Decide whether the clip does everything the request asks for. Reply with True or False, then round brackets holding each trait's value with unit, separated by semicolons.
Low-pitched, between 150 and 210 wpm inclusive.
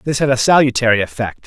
True (125 Hz; 205 wpm)